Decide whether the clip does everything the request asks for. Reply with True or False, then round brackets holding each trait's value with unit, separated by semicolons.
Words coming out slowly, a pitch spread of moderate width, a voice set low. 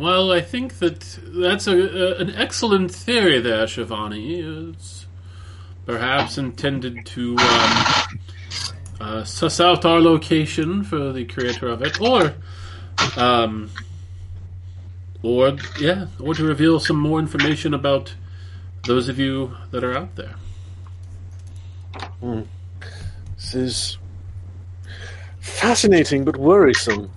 False (115 wpm; 8.3 semitones; 110 Hz)